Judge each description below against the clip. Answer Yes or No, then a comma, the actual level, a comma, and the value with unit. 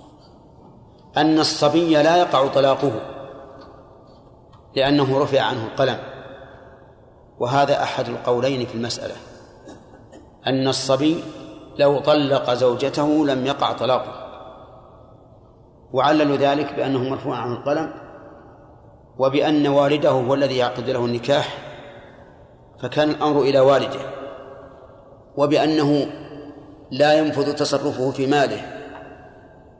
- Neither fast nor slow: Yes, average, 90 wpm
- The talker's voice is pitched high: No, low, 135 Hz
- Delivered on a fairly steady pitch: Yes, narrow, 2.0 semitones